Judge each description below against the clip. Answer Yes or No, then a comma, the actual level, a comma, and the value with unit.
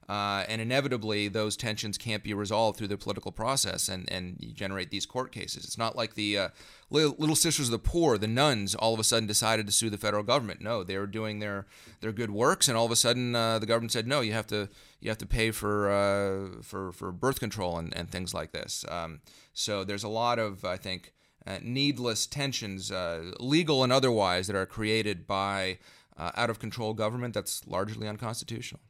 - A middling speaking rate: No, fast, 220 wpm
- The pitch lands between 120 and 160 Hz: No, low, 110 Hz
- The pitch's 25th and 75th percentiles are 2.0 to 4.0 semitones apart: Yes, average, 2.8 semitones